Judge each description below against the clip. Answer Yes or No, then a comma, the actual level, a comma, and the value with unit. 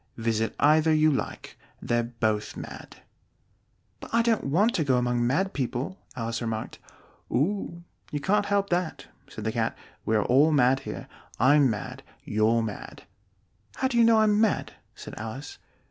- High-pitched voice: No, medium, 140 Hz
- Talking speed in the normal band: Yes, average, 160 wpm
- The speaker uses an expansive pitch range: Yes, wide, 8.3 semitones